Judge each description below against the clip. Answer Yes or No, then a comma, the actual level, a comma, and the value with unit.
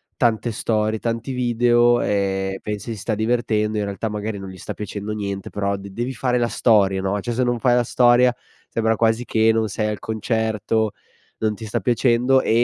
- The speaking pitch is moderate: No, low, 110 Hz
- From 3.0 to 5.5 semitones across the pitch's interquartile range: No, narrow, 2.5 semitones